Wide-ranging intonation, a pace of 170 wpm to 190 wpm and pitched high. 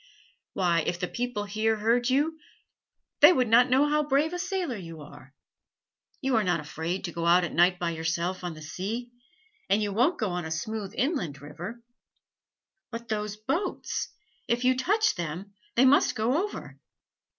Yes: wide, 6.7 semitones; average, 180 wpm; high, 215 Hz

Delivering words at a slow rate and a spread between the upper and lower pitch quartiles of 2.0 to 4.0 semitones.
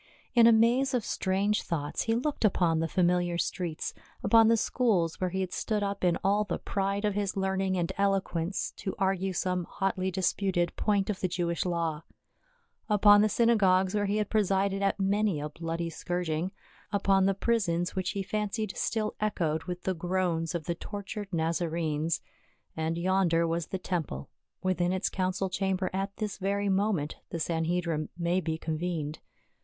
No: average, 170 wpm; average, 2.9 semitones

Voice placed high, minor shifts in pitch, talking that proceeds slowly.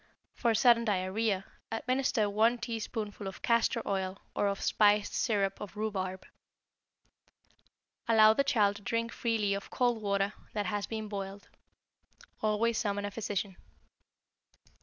Yes: high, 210 Hz; narrow, 2.3 semitones; slow, 130 wpm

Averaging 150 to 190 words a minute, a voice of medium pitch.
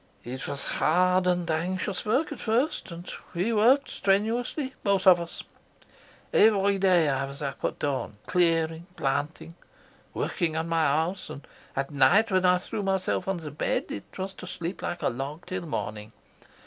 Yes: average, 170 wpm; medium, 175 Hz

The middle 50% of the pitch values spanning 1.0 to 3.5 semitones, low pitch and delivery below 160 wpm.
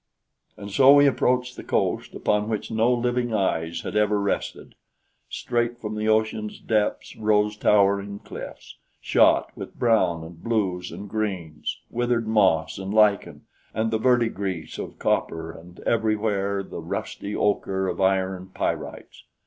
Yes: average, 2.8 semitones; low, 105 Hz; average, 140 wpm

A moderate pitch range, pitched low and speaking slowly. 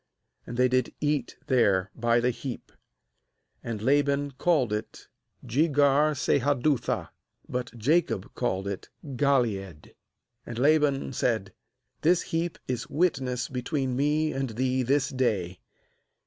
Yes: average, 3.5 semitones; low, 130 Hz; slow, 120 wpm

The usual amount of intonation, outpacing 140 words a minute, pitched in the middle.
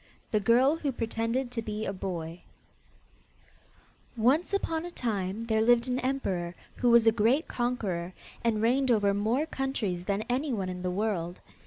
No: average, 4.3 semitones; average, 160 wpm; high, 225 Hz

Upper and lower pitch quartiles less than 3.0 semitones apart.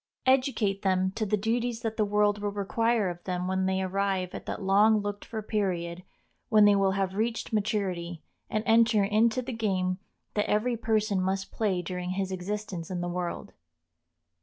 Yes: narrow, 2.6 semitones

